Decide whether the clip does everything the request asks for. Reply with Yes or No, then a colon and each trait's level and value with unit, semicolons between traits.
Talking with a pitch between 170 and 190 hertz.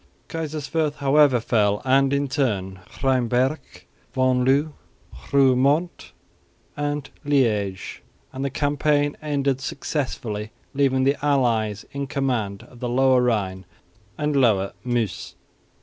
No: low, 135 Hz